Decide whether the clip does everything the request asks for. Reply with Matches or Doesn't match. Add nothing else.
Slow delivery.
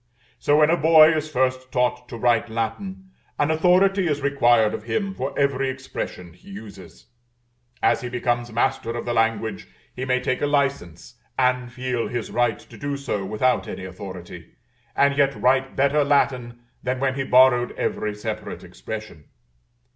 Doesn't match